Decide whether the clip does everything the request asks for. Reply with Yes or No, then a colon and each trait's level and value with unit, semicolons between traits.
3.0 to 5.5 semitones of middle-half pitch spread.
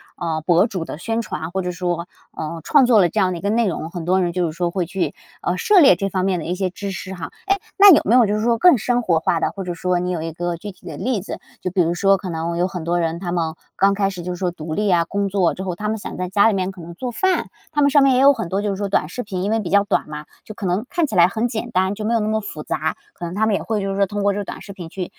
Yes: average, 3.5 semitones